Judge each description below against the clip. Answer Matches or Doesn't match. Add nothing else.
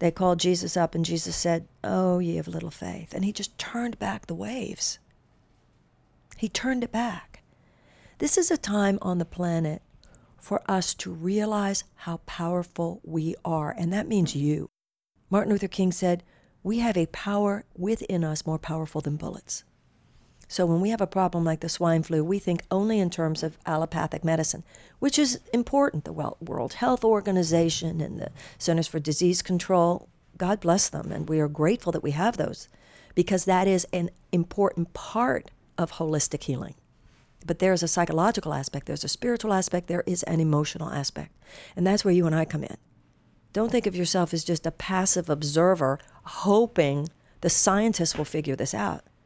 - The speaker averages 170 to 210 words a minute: Matches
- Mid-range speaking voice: Matches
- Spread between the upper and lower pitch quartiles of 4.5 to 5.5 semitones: Doesn't match